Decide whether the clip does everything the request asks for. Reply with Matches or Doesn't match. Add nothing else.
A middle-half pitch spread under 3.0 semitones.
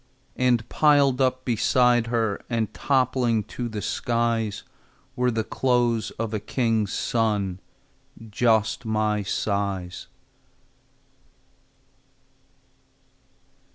Matches